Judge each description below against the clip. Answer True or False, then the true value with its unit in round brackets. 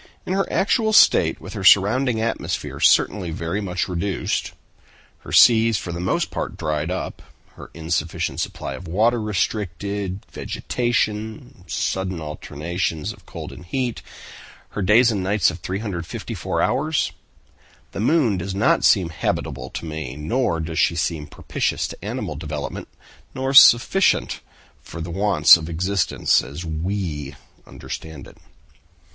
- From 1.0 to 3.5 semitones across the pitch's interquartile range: False (4.9 semitones)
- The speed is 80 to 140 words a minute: True (135 wpm)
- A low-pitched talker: True (95 Hz)